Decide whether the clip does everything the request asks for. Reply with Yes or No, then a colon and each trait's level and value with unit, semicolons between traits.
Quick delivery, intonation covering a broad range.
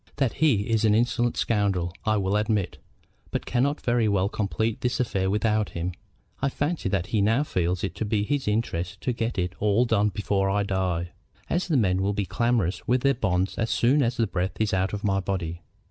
No: fast, 215 wpm; average, 3.7 semitones